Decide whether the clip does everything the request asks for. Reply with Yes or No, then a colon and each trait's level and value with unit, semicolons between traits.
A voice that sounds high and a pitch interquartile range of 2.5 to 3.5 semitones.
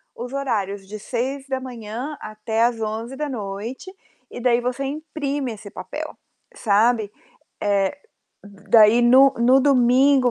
No: high, 240 Hz; average, 3.9 semitones